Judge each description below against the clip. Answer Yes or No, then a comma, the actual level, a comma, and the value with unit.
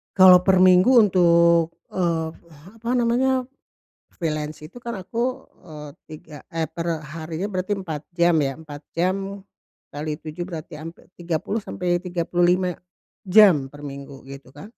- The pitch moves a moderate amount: Yes, average, 3.4 semitones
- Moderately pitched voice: Yes, medium, 170 Hz